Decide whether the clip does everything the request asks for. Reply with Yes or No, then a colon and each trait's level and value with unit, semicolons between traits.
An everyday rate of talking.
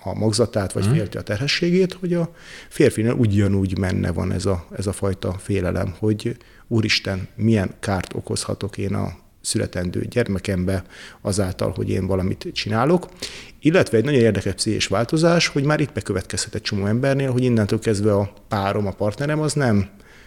No: fast, 160 wpm